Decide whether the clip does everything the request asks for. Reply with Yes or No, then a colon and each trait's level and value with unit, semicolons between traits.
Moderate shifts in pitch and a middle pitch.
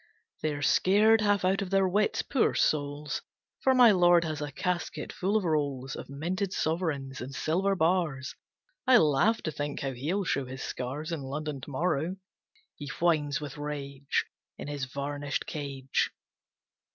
Yes: average, 4.7 semitones; medium, 150 Hz